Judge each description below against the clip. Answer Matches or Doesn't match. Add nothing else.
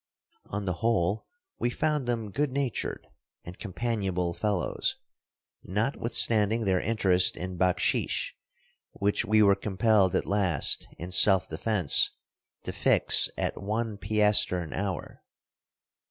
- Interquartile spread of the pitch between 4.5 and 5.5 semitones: Doesn't match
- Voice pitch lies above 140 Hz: Doesn't match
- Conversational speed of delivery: Doesn't match